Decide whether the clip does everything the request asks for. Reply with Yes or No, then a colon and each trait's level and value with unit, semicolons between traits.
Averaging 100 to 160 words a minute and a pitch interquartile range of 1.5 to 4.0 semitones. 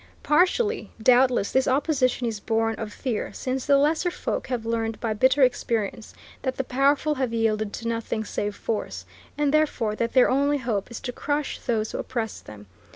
No: average, 180 wpm; average, 3.6 semitones